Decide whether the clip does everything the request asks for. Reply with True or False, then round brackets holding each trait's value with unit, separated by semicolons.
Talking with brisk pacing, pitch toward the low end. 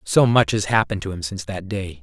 True (265 wpm; 100 Hz)